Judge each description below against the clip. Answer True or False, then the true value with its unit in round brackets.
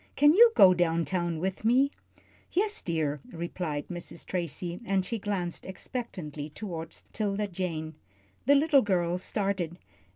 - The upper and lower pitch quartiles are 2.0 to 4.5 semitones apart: True (3.8 semitones)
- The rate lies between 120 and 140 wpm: True (135 wpm)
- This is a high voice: False (180 Hz)